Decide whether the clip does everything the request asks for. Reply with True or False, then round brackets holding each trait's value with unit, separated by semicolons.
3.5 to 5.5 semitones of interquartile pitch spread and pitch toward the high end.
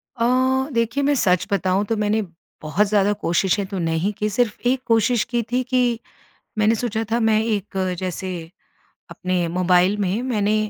True (3.8 semitones; 210 Hz)